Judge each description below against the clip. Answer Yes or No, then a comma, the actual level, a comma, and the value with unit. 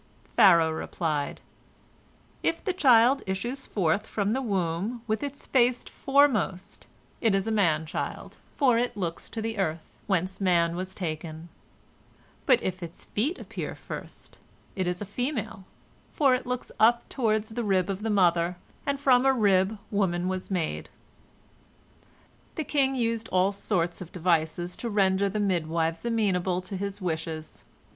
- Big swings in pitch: No, average, 4.8 semitones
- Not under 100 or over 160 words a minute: Yes, average, 150 wpm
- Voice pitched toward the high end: Yes, high, 195 Hz